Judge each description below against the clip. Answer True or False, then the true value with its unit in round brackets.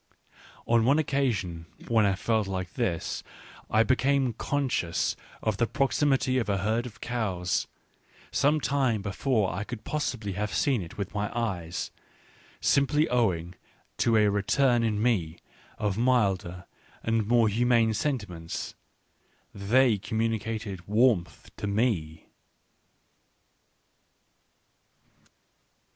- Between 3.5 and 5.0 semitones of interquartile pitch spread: True (4.1 semitones)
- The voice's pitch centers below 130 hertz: True (110 Hz)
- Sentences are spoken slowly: True (115 wpm)